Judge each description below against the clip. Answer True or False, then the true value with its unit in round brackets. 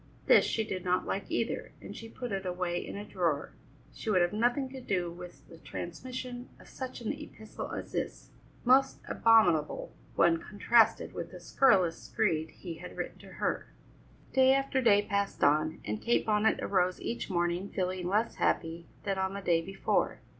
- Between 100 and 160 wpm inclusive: False (180 wpm)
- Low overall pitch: False (195 Hz)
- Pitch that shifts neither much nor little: True (4.9 semitones)